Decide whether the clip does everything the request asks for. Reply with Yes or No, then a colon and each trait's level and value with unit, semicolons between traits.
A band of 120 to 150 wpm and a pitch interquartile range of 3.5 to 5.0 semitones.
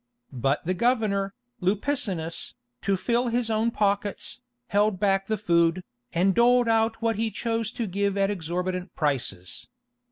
Yes: average, 140 wpm; average, 3.8 semitones